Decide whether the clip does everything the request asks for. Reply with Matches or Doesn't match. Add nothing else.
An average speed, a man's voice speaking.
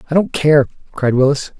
Matches